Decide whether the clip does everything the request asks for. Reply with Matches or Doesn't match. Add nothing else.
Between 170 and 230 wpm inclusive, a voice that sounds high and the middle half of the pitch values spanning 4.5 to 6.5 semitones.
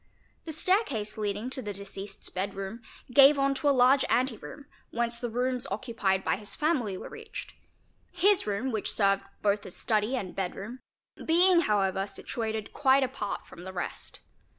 Matches